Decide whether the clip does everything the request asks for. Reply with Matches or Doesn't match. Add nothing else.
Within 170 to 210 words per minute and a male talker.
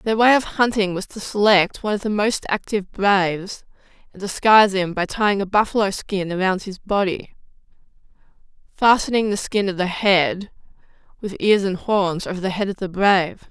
Doesn't match